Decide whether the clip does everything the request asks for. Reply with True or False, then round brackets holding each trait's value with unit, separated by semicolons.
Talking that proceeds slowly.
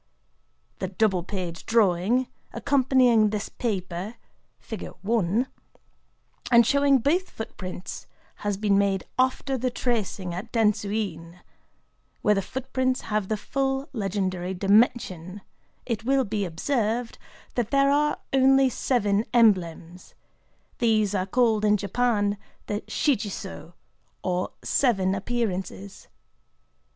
True (110 wpm)